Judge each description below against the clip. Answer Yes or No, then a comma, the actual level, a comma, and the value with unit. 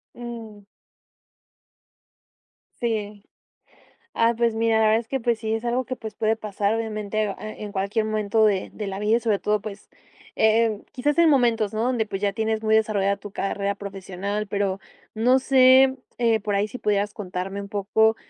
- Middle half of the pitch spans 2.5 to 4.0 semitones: No, narrow, 2.0 semitones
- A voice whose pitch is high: Yes, high, 215 Hz